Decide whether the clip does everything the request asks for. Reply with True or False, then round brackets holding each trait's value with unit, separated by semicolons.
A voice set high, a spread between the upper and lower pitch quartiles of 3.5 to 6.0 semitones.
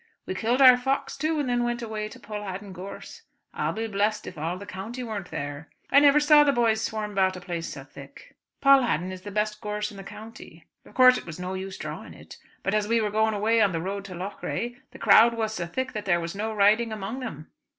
True (210 Hz; 3.9 semitones)